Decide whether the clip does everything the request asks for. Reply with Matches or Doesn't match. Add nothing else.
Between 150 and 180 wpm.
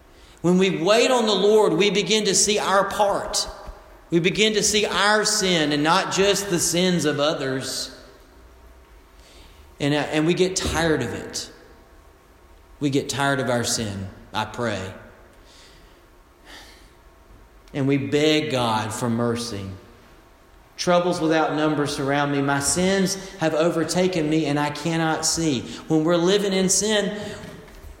Doesn't match